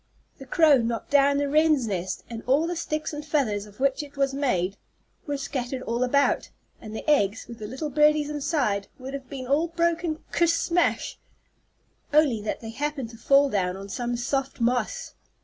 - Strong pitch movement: No, average, 4.3 semitones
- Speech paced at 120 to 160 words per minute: No, average, 185 wpm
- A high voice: Yes, very high, 275 Hz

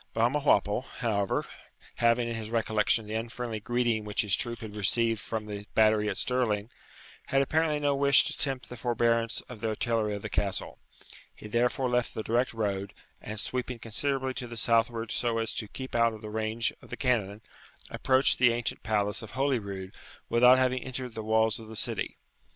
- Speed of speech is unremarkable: Yes, average, 185 wpm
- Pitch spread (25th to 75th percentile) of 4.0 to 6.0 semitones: No, narrow, 2.4 semitones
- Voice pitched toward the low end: Yes, low, 115 Hz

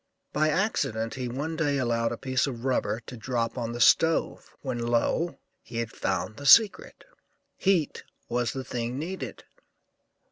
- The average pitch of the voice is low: Yes, low, 130 Hz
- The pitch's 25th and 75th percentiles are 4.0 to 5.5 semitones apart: Yes, average, 4.3 semitones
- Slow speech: No, average, 155 wpm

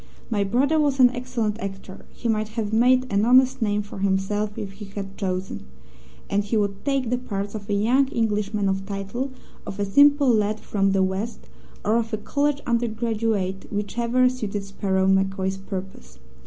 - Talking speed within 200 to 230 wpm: No, average, 175 wpm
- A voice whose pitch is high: Yes, high, 210 Hz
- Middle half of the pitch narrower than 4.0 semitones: Yes, average, 3.5 semitones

